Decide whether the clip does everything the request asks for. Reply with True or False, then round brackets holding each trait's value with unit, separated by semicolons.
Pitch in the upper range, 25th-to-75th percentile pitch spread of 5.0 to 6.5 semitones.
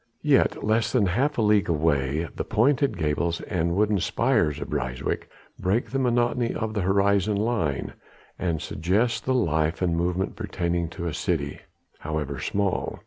False (90 Hz; 5.5 semitones)